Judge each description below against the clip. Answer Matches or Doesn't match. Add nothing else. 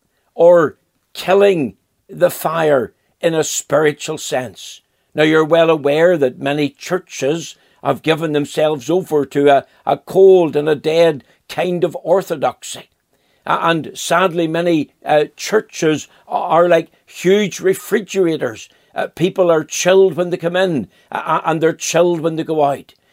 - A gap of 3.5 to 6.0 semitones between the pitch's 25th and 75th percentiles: Doesn't match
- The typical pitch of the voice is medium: Matches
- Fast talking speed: Doesn't match